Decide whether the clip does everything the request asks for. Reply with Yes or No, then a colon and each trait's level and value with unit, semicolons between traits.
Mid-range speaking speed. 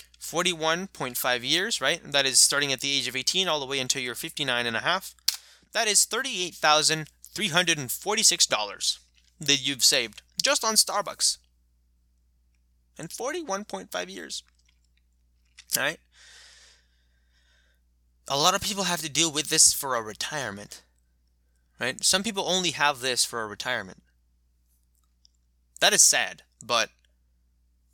No: slow, 125 wpm